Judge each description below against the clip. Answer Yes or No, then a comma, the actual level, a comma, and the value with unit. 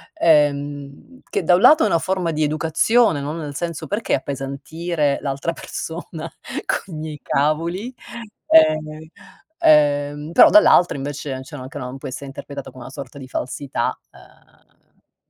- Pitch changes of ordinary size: Yes, average, 3.0 semitones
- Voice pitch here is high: No, medium, 150 Hz